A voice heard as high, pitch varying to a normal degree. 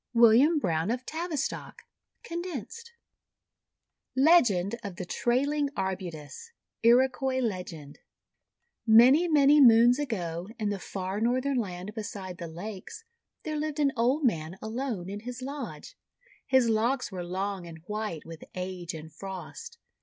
No: high, 225 Hz; wide, 6.8 semitones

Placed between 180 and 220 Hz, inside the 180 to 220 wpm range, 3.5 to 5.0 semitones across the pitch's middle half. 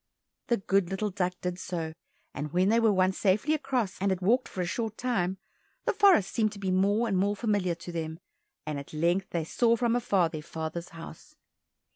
Yes: high, 190 Hz; fast, 205 wpm; average, 4.4 semitones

